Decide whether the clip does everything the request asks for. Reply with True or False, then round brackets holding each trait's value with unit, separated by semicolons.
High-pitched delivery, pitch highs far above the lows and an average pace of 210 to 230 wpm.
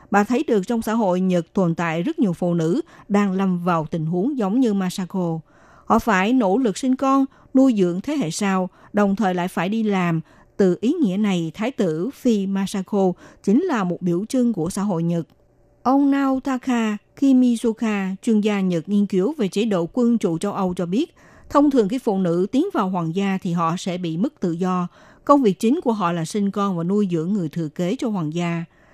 False (200 Hz; 4.9 semitones; 220 wpm)